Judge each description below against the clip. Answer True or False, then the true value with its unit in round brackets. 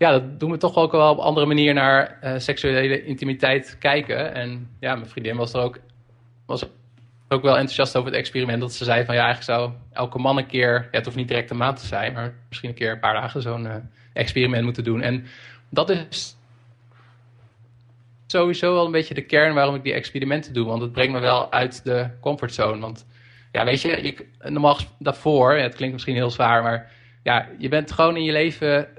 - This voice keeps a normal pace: False (215 wpm)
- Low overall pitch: True (125 Hz)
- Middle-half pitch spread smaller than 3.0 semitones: True (2.6 semitones)